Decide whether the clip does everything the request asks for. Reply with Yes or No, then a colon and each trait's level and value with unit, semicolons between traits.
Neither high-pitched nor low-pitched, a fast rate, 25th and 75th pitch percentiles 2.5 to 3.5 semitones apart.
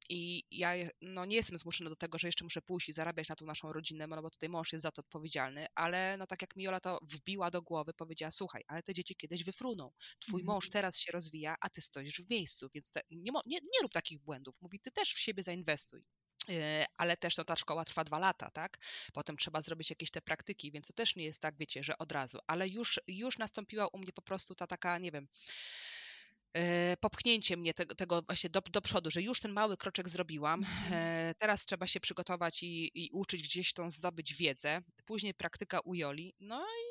Yes: medium, 175 Hz; fast, 215 wpm; average, 3.1 semitones